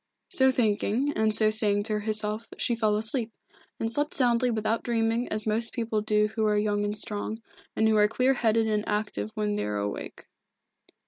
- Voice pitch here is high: Yes, high, 220 Hz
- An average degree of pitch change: No, narrow, 1.6 semitones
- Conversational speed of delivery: Yes, average, 190 wpm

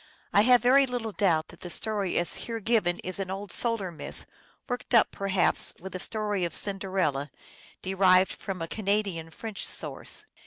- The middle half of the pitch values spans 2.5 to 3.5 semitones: Yes, average, 3.1 semitones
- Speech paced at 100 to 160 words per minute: No, average, 170 wpm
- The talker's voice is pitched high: Yes, high, 195 Hz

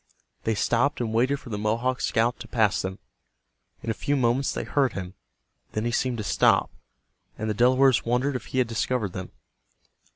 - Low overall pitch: Yes, low, 120 Hz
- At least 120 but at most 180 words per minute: No, average, 190 wpm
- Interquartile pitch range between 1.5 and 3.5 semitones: Yes, average, 2.9 semitones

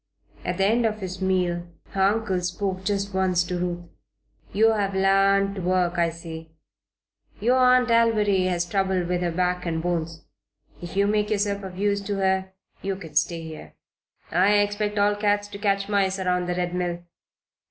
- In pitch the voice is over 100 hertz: Yes, high, 190 Hz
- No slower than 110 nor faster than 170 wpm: No, average, 180 wpm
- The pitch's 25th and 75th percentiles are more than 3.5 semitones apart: No, narrow, 2.4 semitones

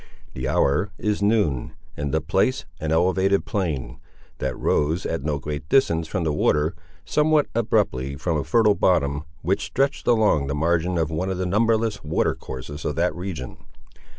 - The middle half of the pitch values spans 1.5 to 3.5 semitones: No, wide, 5.6 semitones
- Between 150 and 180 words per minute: Yes, average, 170 wpm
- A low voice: Yes, very low, 85 Hz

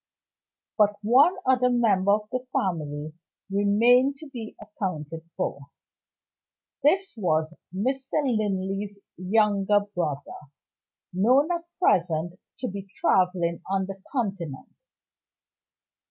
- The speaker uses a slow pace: Yes, slow, 100 wpm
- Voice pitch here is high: Yes, high, 200 Hz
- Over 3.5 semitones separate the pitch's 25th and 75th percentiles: Yes, average, 5.3 semitones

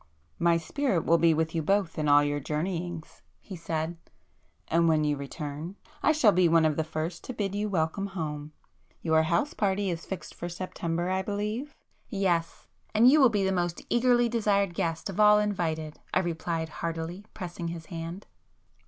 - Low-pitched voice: No, medium, 170 Hz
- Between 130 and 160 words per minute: No, average, 175 wpm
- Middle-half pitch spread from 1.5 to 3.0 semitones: No, average, 3.7 semitones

